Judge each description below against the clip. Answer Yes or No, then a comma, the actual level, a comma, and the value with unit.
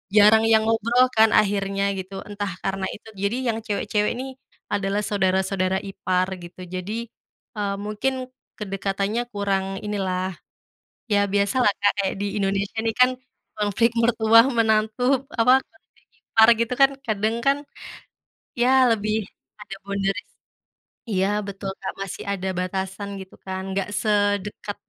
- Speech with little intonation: Yes, narrow, 2.1 semitones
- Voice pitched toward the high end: Yes, high, 205 Hz